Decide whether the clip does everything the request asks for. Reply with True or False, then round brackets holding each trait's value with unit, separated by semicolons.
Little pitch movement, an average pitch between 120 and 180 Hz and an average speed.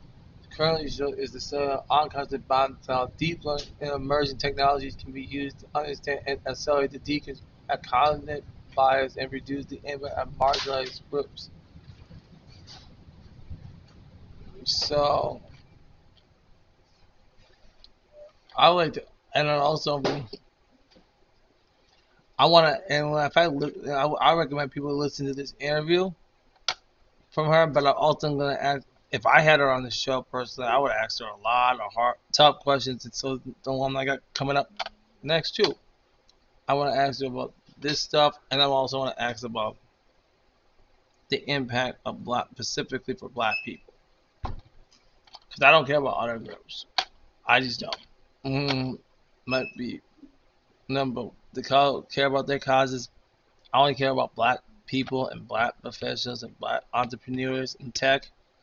True (2.0 semitones; 135 Hz; 150 wpm)